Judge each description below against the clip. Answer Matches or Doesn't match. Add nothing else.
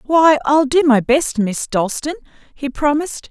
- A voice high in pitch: Matches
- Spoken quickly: Doesn't match